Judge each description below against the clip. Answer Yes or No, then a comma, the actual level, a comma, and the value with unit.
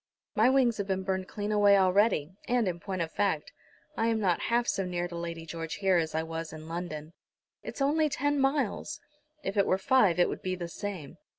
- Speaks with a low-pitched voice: No, high, 190 Hz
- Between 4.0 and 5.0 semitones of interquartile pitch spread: Yes, average, 4.6 semitones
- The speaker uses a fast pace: Yes, fast, 215 wpm